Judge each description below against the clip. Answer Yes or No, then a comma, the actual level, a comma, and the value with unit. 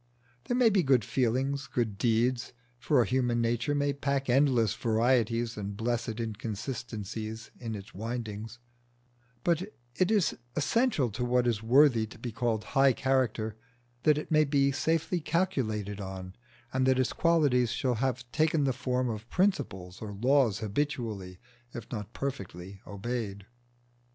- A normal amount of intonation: Yes, average, 4.0 semitones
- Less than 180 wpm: Yes, average, 145 wpm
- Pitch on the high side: No, low, 120 Hz